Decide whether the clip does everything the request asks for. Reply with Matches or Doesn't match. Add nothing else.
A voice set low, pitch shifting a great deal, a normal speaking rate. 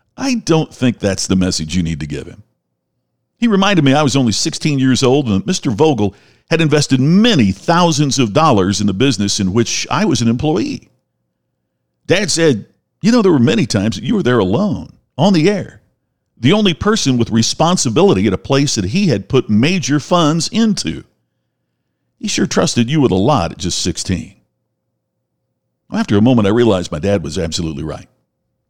Matches